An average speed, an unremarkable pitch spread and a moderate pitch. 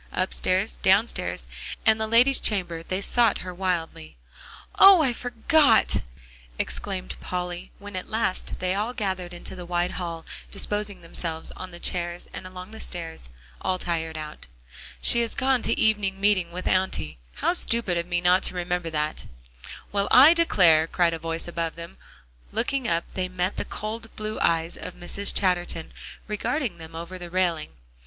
Yes: average, 165 wpm; average, 3.7 semitones; medium, 180 Hz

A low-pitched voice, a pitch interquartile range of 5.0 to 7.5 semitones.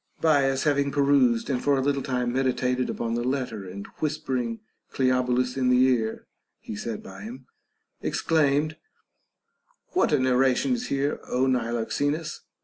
No: low, 130 Hz; narrow, 2.5 semitones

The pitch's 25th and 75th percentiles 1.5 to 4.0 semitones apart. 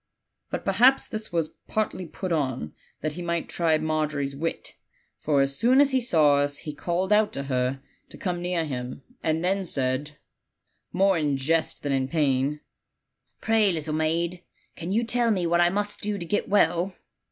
No: average, 4.8 semitones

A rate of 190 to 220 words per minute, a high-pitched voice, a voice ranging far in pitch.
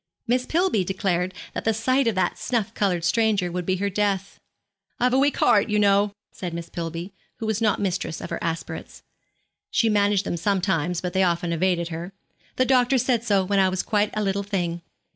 No: average, 200 wpm; high, 195 Hz; average, 3.6 semitones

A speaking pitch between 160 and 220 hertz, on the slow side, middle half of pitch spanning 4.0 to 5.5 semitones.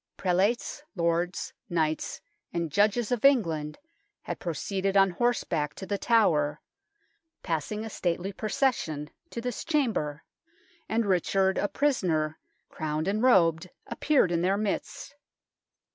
Yes: high, 190 Hz; slow, 125 wpm; average, 5.2 semitones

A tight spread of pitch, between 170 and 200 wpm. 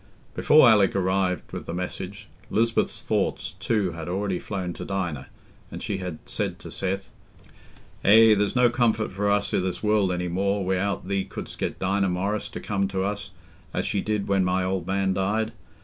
Yes: narrow, 1.8 semitones; average, 185 wpm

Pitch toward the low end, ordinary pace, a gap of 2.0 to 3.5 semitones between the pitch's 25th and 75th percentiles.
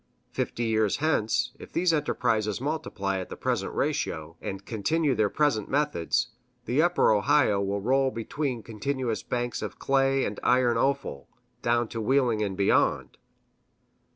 No: low, 120 Hz; average, 145 wpm; average, 4.6 semitones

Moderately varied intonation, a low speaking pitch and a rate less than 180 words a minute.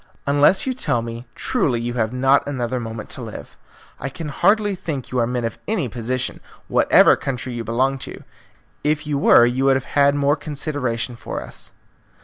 No: average, 3.3 semitones; low, 130 Hz; average, 185 wpm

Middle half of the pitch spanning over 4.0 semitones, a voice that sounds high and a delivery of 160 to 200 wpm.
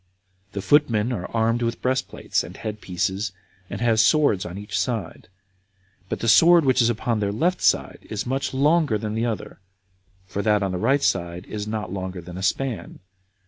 No: average, 4.4 semitones; low, 110 Hz; average, 185 wpm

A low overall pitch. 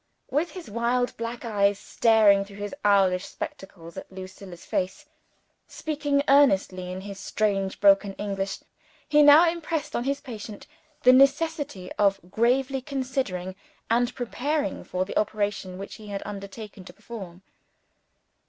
No: high, 210 Hz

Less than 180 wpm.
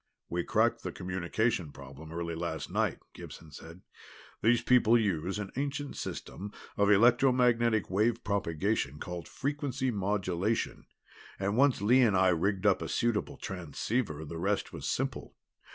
Yes: average, 140 wpm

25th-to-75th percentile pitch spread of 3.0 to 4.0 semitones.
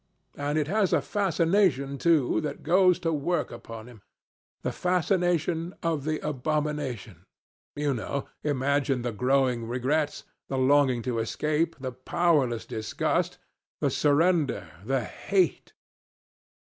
No: average, 4.5 semitones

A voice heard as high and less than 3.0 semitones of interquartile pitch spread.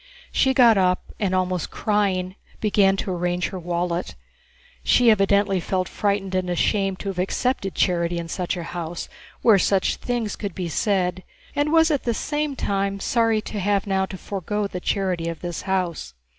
Yes: high, 195 Hz; narrow, 2.6 semitones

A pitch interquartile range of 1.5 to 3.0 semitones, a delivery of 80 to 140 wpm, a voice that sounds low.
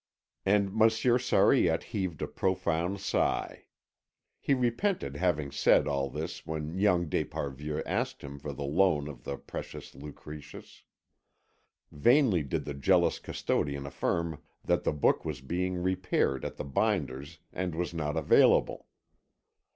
No: average, 4.7 semitones; slow, 135 wpm; very low, 80 Hz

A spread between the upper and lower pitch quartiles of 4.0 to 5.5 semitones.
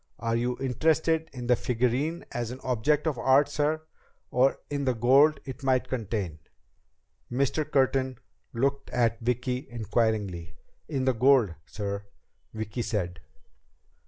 No: average, 3.4 semitones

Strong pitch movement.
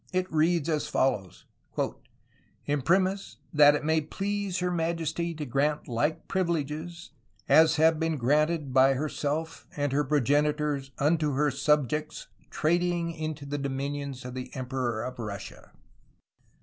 No: average, 2.9 semitones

